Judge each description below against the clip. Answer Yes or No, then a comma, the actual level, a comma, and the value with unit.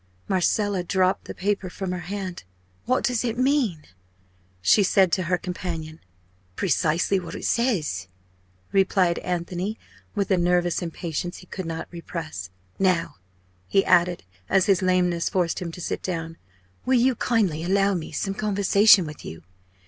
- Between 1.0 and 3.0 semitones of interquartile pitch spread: Yes, average, 2.7 semitones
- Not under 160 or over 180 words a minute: No, average, 150 wpm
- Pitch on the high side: No, medium, 180 Hz